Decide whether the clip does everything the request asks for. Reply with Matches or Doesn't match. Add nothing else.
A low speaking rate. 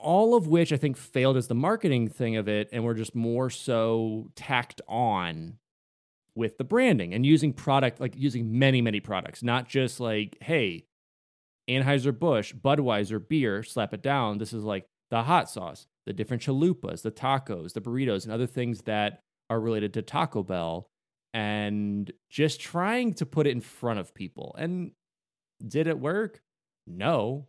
Doesn't match